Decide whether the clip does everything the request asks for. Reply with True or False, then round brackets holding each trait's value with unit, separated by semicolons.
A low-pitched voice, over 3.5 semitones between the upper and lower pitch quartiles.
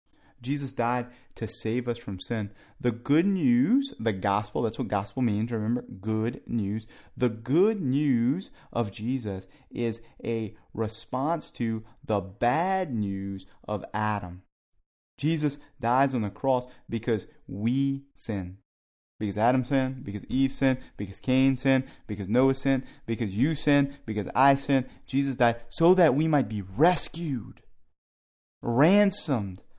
True (120 Hz; 4.4 semitones)